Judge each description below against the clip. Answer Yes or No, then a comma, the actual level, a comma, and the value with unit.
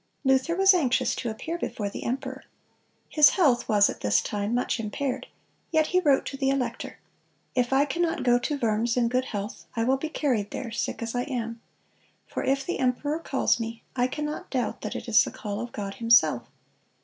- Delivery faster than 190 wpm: Yes, average, 200 wpm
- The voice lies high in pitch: Yes, very high, 250 Hz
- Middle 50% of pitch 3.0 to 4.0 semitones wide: Yes, average, 3.7 semitones